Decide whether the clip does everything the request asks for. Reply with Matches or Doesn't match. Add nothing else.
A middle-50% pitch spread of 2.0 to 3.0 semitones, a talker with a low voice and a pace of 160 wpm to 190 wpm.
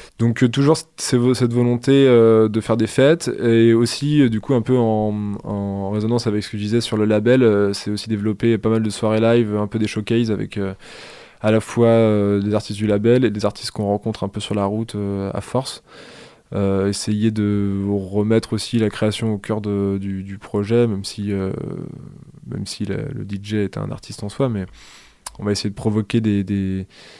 Doesn't match